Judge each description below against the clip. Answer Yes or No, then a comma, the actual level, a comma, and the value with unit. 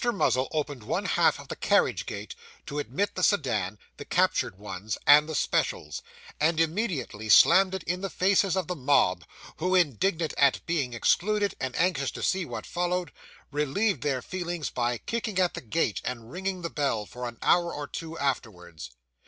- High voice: No, medium, 155 Hz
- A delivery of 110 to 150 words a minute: No, average, 175 wpm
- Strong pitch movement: Yes, wide, 6.4 semitones